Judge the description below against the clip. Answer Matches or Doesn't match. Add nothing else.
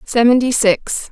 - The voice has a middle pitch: Doesn't match